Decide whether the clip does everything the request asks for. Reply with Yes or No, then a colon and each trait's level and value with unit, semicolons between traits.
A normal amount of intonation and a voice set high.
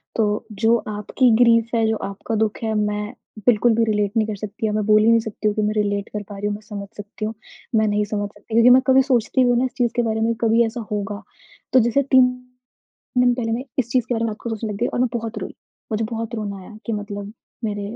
No: narrow, 2.1 semitones; high, 220 Hz